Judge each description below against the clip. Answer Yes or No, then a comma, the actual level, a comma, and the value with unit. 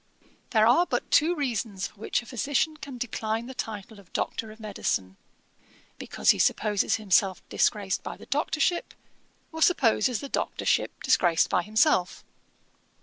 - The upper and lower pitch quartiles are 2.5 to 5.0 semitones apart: No, wide, 5.4 semitones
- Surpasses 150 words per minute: No, average, 145 wpm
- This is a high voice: Yes, high, 225 Hz